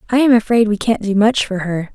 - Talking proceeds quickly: Yes, fast, 280 wpm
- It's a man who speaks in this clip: No, female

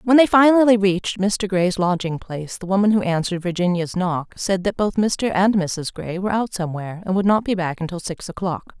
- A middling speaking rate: No, fast, 220 wpm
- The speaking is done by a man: No, female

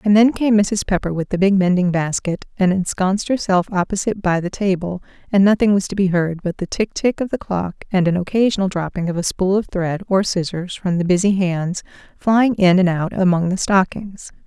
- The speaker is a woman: Yes, female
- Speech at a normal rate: No, fast, 215 wpm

